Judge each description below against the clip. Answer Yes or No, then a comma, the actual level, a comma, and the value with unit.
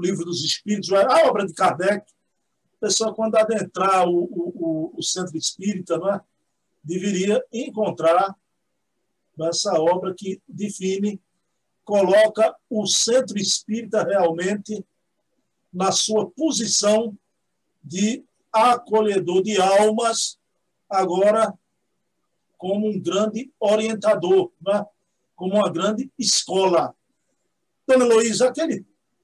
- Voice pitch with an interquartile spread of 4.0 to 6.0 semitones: No, average, 3.0 semitones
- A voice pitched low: No, high, 200 Hz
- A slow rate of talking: Yes, slow, 105 wpm